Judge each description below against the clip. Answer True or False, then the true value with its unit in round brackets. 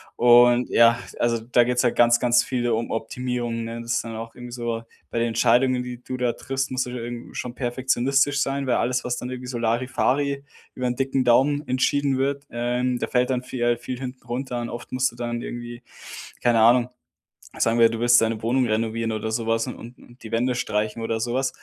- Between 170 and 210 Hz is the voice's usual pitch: False (120 Hz)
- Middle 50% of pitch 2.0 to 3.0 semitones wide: False (1.4 semitones)